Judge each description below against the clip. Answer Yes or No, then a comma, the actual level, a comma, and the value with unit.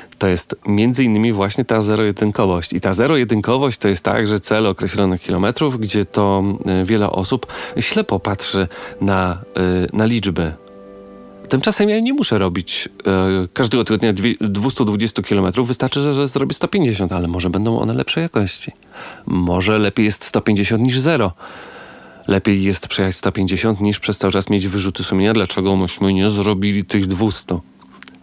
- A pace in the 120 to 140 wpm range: No, average, 155 wpm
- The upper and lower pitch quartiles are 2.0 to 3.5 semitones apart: Yes, average, 2.9 semitones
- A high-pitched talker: No, low, 100 Hz